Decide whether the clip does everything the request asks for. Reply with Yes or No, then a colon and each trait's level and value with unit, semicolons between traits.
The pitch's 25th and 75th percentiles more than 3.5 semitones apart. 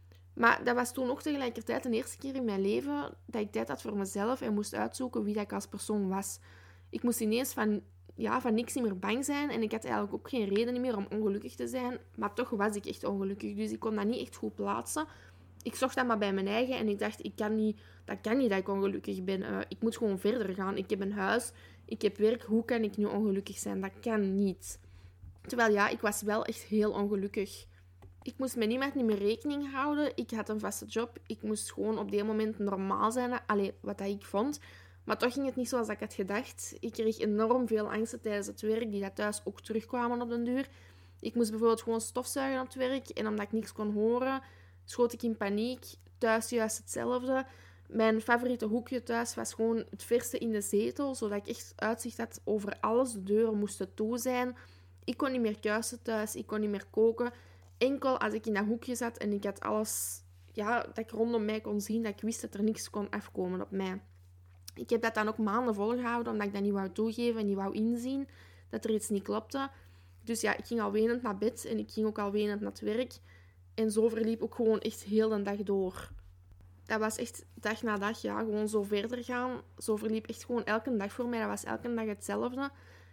No: average, 2.9 semitones